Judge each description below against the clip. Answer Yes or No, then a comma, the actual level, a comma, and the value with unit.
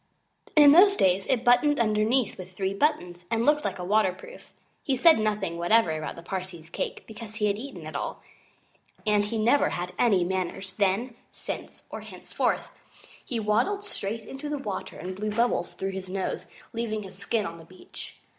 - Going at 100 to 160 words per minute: No, average, 185 wpm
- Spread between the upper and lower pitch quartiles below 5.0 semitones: Yes, average, 4.3 semitones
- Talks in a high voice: Yes, high, 210 Hz